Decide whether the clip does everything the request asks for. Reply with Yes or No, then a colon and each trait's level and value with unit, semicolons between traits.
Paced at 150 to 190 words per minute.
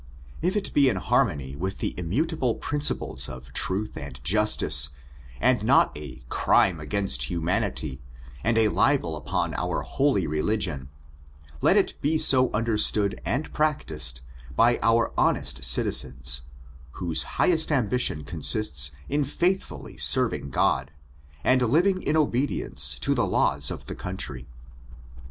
No: slow, 135 wpm